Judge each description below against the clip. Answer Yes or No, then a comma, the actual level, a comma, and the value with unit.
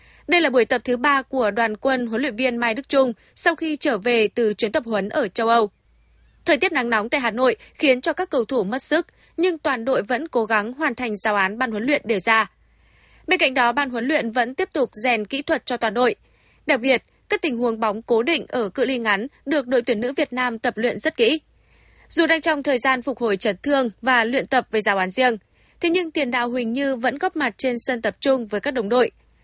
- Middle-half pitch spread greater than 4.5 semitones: No, average, 3.9 semitones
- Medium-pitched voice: No, very high, 255 Hz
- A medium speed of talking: No, fast, 255 wpm